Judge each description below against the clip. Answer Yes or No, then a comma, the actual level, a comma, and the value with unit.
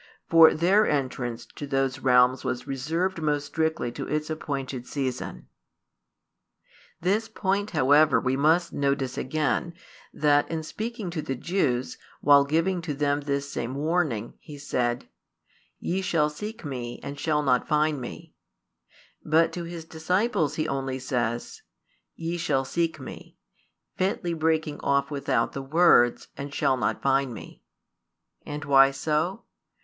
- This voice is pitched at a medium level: Yes, medium, 145 Hz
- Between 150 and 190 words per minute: No, average, 140 wpm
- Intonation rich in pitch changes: No, average, 3.6 semitones